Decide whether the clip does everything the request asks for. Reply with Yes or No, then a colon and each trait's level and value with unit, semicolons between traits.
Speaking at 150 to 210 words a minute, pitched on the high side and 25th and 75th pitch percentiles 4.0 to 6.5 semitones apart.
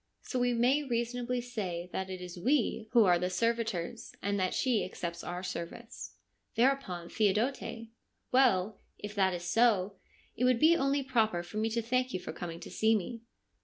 Yes: average, 185 wpm; high, 220 Hz; average, 5.1 semitones